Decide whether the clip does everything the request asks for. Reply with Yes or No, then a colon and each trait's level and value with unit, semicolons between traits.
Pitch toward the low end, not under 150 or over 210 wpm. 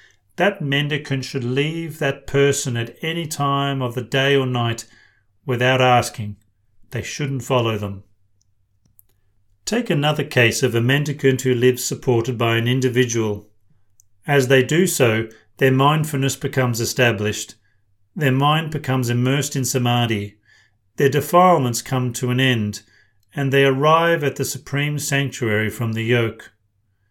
No: low, 125 Hz; slow, 135 wpm